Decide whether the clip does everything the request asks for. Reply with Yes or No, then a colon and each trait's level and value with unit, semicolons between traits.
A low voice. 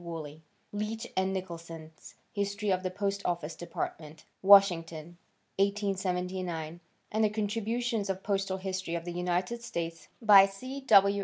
No: high, 190 Hz